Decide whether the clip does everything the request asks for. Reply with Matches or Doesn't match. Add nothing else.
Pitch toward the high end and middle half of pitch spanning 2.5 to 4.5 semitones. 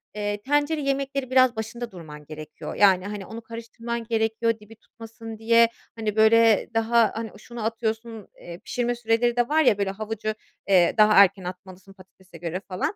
Matches